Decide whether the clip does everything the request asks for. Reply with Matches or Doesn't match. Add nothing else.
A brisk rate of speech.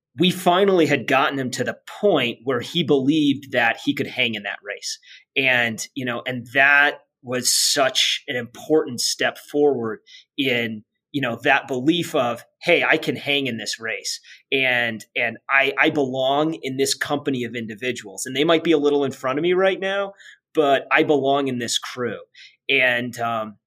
Doesn't match